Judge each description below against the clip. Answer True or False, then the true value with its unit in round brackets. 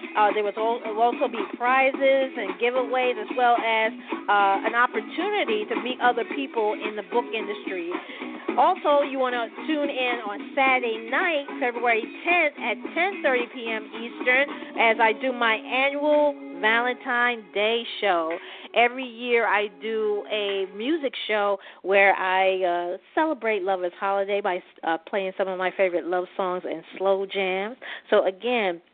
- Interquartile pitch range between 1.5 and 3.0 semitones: False (5.2 semitones)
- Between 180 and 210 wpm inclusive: False (150 wpm)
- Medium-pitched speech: False (235 Hz)